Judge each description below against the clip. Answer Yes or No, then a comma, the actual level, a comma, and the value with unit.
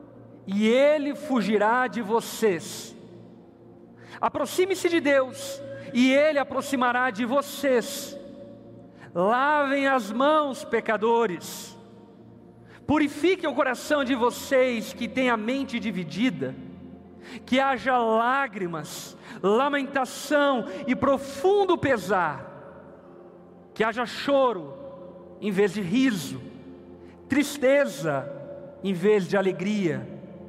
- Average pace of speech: No, slow, 90 wpm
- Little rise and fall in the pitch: No, average, 4.7 semitones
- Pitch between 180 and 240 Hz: No, very high, 255 Hz